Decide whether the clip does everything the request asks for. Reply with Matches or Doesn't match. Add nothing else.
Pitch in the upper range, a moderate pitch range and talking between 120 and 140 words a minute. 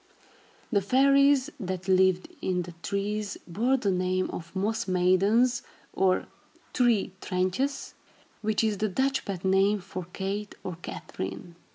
Matches